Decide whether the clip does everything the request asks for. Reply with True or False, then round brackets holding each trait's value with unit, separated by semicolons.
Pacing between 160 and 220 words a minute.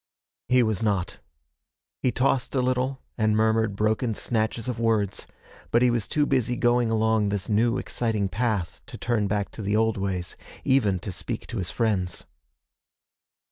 True (165 wpm)